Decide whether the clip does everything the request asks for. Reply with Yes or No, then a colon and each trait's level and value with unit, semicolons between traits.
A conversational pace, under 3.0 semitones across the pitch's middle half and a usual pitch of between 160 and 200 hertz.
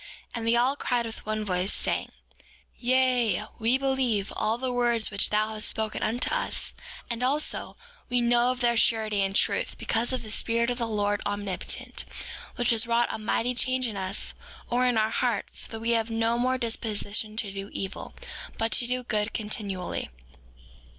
No: average, 185 wpm; narrow, 2.4 semitones; high, 230 Hz